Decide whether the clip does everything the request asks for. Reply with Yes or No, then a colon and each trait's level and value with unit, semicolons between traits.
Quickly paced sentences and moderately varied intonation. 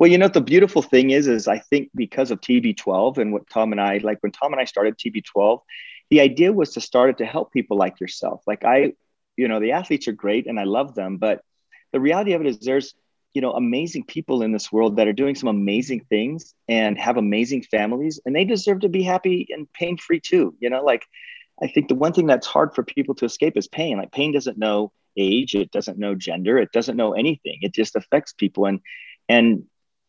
No: fast, 230 wpm; wide, 7.1 semitones